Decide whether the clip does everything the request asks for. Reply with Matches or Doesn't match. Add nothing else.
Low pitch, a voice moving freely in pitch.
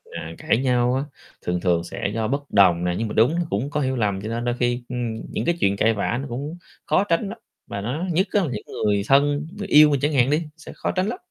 Matches